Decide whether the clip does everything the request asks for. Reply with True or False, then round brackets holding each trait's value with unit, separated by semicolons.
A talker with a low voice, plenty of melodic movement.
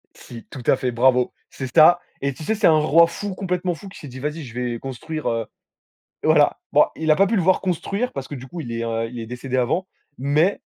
False (145 Hz; 5.9 semitones)